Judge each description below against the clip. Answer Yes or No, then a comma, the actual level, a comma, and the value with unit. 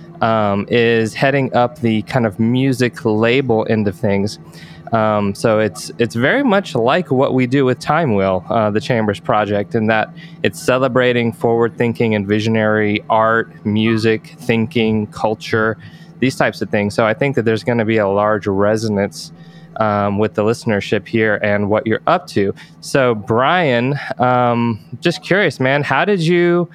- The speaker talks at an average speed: Yes, average, 170 wpm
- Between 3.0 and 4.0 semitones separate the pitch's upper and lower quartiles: Yes, average, 3.5 semitones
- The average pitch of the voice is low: Yes, low, 115 Hz